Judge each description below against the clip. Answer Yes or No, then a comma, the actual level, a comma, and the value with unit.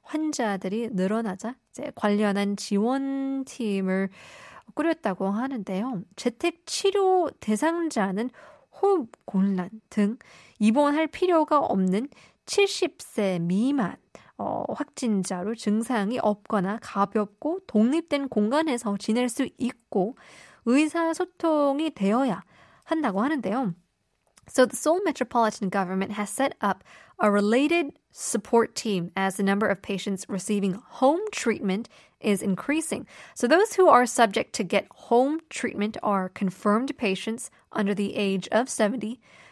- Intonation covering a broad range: Yes, wide, 5.9 semitones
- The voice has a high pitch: Yes, high, 230 Hz